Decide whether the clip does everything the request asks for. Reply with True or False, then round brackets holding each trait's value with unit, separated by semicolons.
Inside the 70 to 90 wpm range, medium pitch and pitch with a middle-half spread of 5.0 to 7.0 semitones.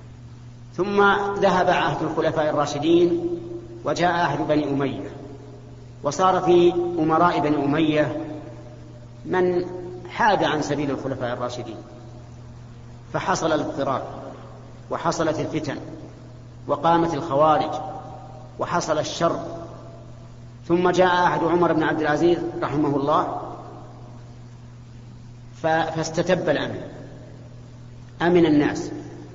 True (85 wpm; 145 Hz; 5.5 semitones)